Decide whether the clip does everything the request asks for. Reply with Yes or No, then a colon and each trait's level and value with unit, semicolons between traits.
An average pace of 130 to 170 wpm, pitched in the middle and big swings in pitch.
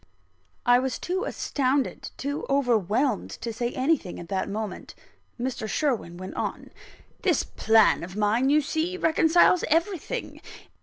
No: slow, 135 wpm; very high, 255 Hz; wide, 6.0 semitones